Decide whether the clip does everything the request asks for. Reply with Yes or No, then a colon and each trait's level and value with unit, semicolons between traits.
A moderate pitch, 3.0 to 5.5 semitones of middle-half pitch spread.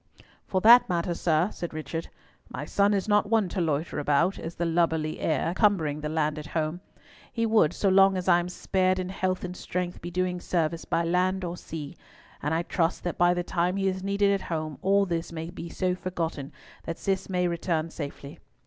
No: medium, 175 Hz; narrow, 2.6 semitones